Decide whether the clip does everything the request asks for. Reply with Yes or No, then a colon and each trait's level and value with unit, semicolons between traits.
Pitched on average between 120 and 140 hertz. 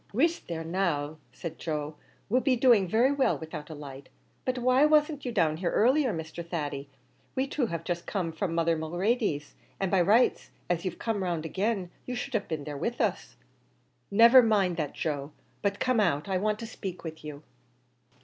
No: medium, 185 Hz